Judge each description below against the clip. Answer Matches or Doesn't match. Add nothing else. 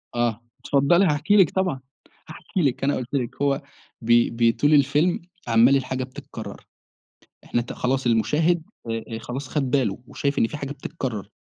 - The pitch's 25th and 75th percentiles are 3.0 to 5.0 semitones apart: Matches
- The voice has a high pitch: Doesn't match